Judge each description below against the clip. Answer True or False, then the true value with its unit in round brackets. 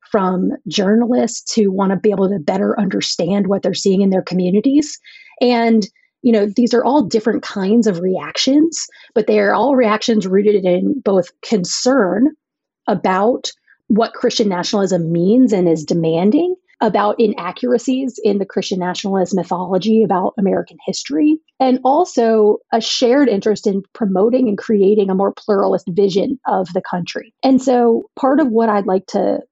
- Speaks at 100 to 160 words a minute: True (155 wpm)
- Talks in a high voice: True (215 Hz)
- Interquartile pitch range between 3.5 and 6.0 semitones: True (4.6 semitones)